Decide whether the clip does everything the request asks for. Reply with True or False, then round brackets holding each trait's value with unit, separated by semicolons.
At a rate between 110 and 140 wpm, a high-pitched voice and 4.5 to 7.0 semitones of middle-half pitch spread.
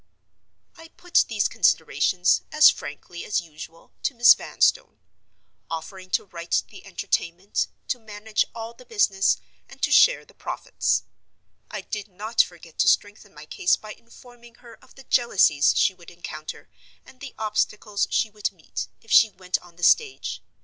False (160 wpm; 205 Hz; 4.8 semitones)